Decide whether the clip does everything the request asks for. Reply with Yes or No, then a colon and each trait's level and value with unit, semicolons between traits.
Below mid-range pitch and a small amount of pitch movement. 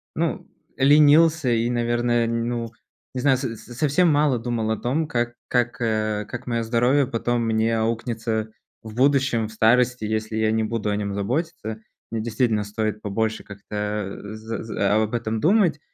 Yes: low, 115 Hz; narrow, 2.3 semitones